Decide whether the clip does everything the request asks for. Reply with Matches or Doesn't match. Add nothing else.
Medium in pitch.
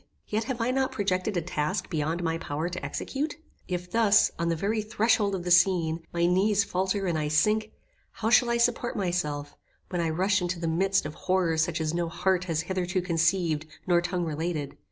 Matches